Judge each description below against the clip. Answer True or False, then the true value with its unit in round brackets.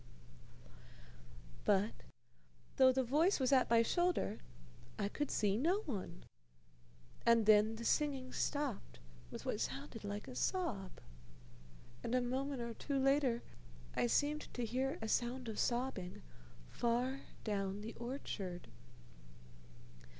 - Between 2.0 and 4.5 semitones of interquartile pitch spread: True (4.2 semitones)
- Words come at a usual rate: False (130 wpm)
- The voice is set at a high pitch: True (240 Hz)